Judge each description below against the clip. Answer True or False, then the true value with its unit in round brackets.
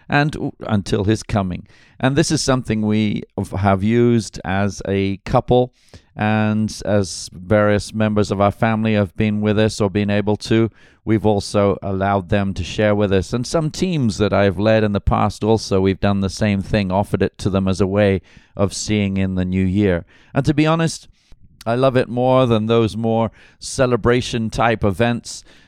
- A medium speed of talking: True (185 wpm)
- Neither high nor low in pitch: False (105 Hz)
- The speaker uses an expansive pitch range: False (2.6 semitones)